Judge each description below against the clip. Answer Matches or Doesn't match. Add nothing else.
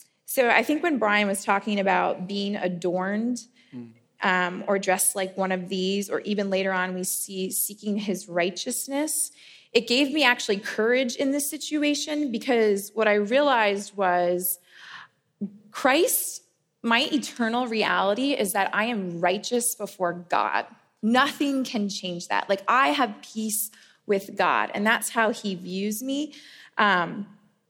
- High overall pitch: Matches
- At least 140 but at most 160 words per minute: Matches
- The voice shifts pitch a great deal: Doesn't match